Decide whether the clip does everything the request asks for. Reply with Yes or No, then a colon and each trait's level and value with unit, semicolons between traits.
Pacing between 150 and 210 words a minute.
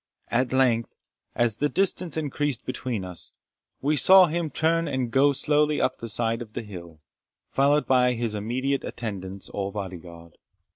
Yes: average, 155 wpm